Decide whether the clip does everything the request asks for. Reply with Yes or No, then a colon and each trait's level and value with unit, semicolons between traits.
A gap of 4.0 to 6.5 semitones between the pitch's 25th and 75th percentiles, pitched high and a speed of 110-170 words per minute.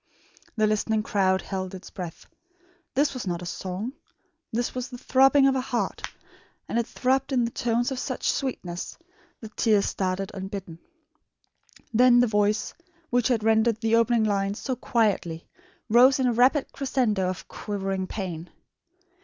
Yes: average, 4.3 semitones; high, 220 Hz; average, 155 wpm